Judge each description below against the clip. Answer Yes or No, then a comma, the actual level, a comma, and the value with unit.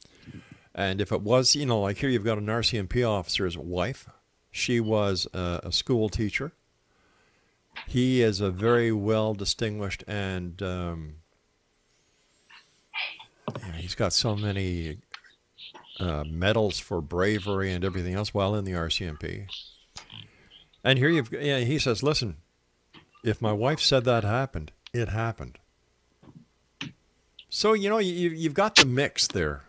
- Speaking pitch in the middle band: No, low, 100 Hz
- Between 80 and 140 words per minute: Yes, slow, 135 wpm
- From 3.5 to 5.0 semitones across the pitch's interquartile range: No, wide, 5.6 semitones